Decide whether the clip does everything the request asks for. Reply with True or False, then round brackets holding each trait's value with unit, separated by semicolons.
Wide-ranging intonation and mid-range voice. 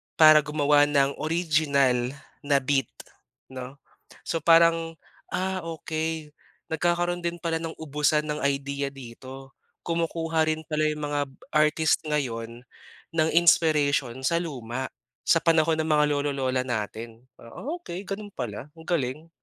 False (3.3 semitones; 150 Hz)